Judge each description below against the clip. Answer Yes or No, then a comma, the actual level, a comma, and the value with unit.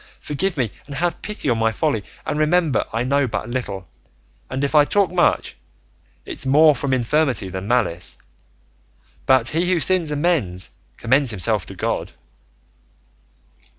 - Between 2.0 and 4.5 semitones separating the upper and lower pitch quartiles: No, wide, 5.6 semitones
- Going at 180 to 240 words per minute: No, average, 150 wpm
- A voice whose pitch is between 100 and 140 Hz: Yes, low, 135 Hz